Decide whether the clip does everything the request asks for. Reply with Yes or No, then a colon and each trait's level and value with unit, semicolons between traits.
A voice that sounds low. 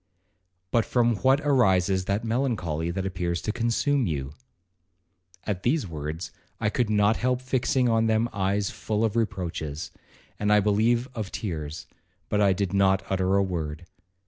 Yes: low, 100 Hz